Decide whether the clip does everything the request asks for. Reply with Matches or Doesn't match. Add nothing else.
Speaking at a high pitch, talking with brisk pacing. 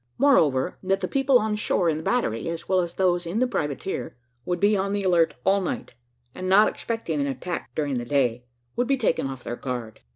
Doesn't match